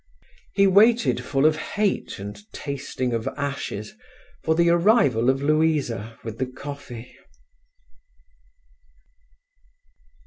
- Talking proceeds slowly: Yes, slow, 100 wpm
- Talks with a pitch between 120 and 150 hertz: Yes, medium, 140 Hz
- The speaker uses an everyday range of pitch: No, wide, 5.8 semitones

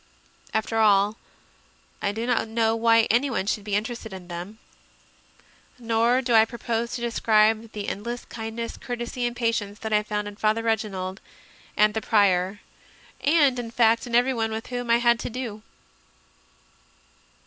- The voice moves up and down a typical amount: No, narrow, 2.0 semitones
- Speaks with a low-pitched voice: No, high, 225 Hz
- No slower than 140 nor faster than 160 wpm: Yes, average, 155 wpm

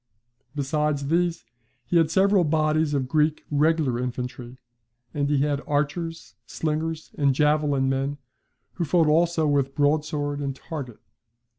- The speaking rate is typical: No, slow, 130 wpm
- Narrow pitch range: Yes, narrow, 2.3 semitones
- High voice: No, medium, 150 Hz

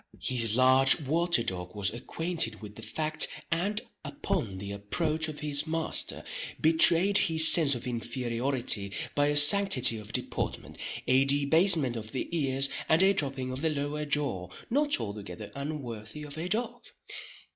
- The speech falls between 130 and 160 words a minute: Yes, average, 150 wpm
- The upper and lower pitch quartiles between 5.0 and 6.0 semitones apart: Yes, wide, 5.5 semitones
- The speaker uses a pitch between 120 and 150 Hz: Yes, medium, 140 Hz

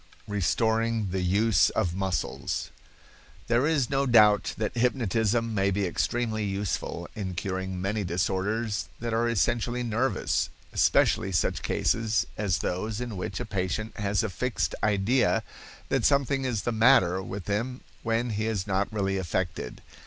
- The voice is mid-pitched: No, low, 105 Hz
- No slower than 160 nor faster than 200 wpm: No, average, 145 wpm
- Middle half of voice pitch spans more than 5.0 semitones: No, average, 3.5 semitones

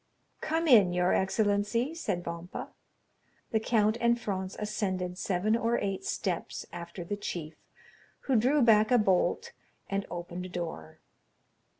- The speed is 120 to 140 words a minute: Yes, slow, 135 wpm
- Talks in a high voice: Yes, high, 200 Hz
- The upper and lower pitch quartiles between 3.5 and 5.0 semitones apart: Yes, average, 4.2 semitones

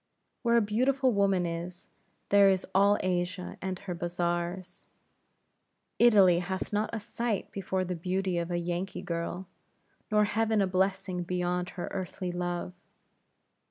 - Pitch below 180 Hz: No, medium, 185 Hz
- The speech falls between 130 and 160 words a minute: Yes, average, 140 wpm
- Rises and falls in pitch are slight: Yes, narrow, 2.3 semitones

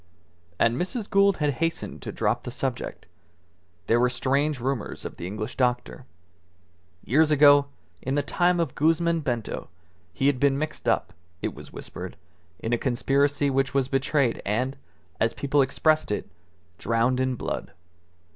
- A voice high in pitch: No, low, 135 Hz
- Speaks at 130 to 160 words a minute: Yes, average, 155 wpm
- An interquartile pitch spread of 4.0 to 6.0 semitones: No, average, 3.6 semitones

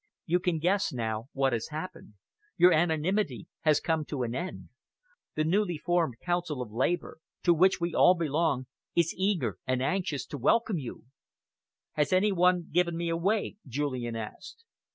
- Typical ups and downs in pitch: Yes, average, 5.0 semitones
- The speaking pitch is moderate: Yes, medium, 165 Hz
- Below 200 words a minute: Yes, average, 160 wpm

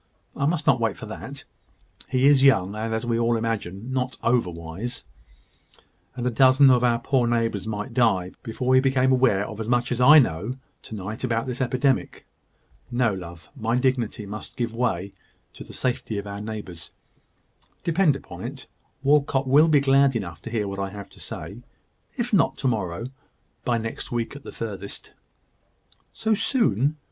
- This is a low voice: Yes, low, 120 Hz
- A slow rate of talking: No, average, 175 wpm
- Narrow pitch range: No, average, 4.0 semitones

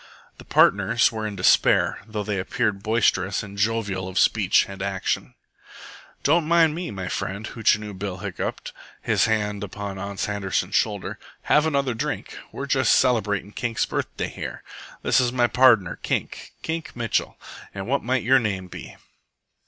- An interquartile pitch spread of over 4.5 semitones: No, average, 3.6 semitones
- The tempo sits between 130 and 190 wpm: Yes, average, 155 wpm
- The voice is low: Yes, low, 105 Hz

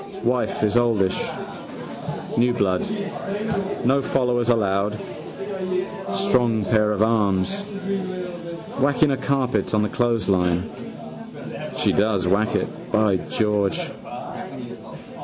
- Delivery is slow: Yes, slow, 95 wpm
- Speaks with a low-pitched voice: Yes, low, 110 Hz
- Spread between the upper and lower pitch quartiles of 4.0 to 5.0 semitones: No, average, 3.3 semitones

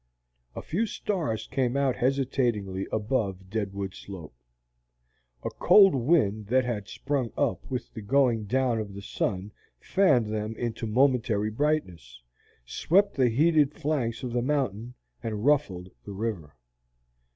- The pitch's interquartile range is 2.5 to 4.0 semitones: No, average, 5.1 semitones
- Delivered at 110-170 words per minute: Yes, slow, 135 wpm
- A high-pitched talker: No, low, 115 Hz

